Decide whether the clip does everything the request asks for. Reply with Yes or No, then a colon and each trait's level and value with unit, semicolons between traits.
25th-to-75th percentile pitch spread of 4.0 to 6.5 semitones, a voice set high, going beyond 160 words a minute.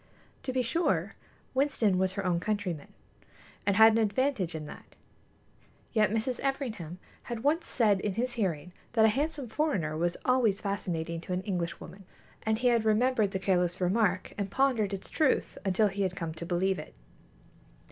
Yes: average, 4.8 semitones; high, 205 Hz; average, 170 wpm